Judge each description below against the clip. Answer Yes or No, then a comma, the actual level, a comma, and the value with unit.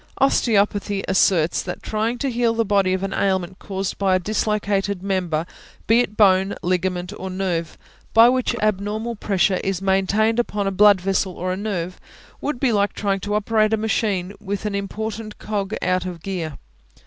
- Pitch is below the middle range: No, high, 200 Hz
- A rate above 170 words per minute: Yes, average, 180 wpm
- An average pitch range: No, narrow, 2.3 semitones